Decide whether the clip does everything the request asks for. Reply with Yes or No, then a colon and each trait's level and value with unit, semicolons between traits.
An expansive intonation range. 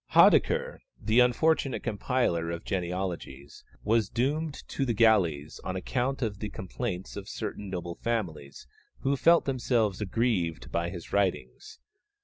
Yes: wide, 6.0 semitones